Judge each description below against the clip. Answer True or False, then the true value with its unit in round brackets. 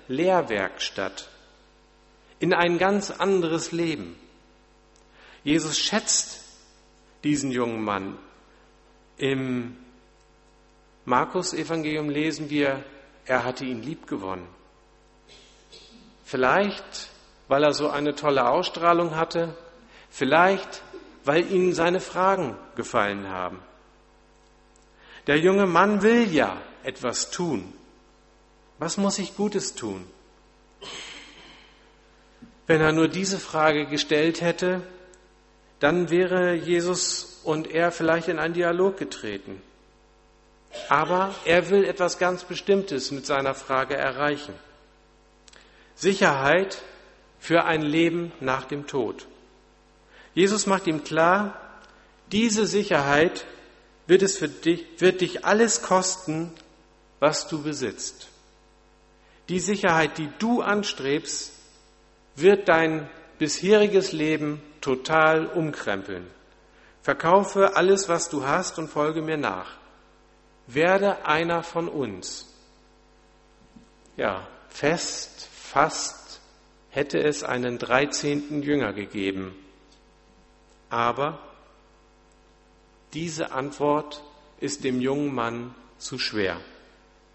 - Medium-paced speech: False (95 wpm)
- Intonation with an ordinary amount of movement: False (5.9 semitones)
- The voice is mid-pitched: True (155 Hz)